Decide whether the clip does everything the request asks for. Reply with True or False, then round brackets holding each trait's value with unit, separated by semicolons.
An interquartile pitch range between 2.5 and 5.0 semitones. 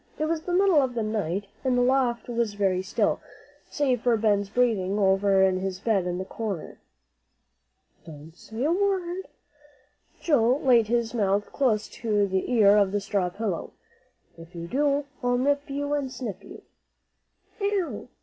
False (5.5 semitones)